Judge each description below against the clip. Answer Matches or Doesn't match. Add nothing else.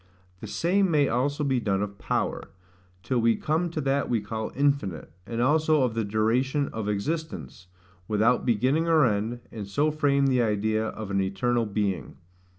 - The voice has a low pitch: Matches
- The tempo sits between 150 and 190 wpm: Matches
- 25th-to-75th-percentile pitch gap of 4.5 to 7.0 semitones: Matches